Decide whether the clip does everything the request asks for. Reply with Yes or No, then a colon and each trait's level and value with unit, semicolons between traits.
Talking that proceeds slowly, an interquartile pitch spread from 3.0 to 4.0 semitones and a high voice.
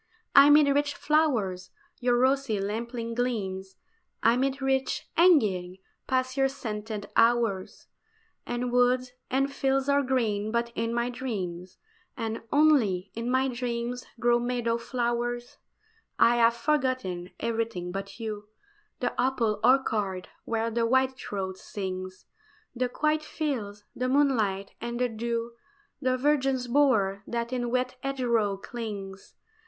Yes: slow, 125 wpm; average, 3.7 semitones; high, 235 Hz